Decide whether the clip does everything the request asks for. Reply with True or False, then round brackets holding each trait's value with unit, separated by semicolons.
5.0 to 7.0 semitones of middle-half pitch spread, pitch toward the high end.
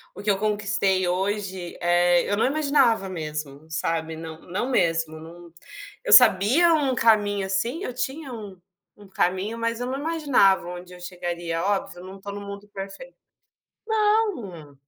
True (5.3 semitones; 195 Hz)